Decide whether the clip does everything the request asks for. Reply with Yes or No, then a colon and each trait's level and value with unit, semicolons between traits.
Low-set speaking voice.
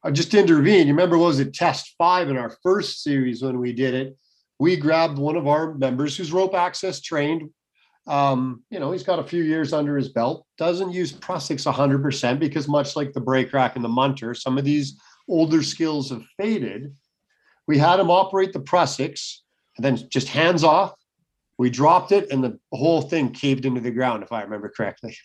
No: medium, 145 Hz